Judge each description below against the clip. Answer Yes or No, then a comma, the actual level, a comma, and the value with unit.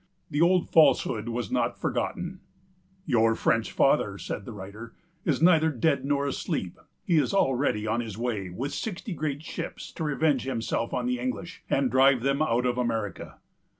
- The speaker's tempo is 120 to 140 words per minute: No, average, 170 wpm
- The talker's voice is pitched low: Yes, low, 130 Hz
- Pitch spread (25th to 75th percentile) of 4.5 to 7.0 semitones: Yes, average, 5.0 semitones